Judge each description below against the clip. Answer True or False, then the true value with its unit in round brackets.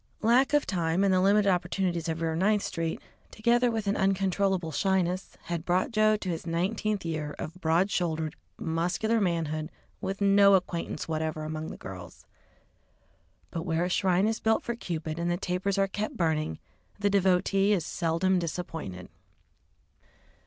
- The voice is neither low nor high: True (180 Hz)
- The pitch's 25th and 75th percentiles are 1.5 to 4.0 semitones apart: True (3.4 semitones)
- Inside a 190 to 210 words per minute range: False (160 wpm)